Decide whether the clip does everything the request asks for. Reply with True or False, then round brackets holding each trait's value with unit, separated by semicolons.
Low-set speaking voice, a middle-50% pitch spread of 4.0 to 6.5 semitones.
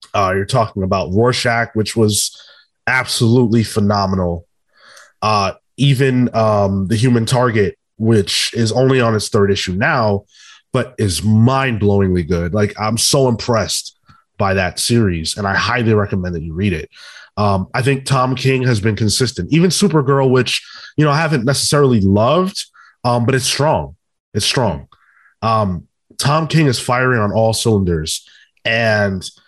True (110 Hz; 4.4 semitones)